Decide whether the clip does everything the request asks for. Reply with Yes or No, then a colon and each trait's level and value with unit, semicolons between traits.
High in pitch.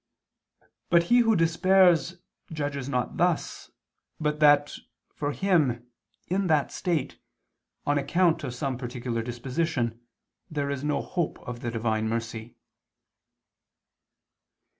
No: medium, 145 Hz